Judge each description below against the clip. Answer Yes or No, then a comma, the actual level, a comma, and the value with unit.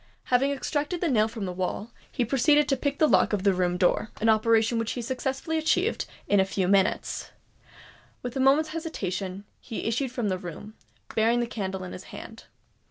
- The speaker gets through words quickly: No, average, 190 wpm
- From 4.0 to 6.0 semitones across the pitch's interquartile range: Yes, wide, 5.5 semitones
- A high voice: Yes, high, 225 Hz